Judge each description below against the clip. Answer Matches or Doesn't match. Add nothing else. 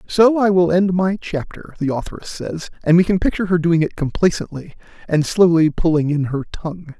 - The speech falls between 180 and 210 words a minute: Matches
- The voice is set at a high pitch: Doesn't match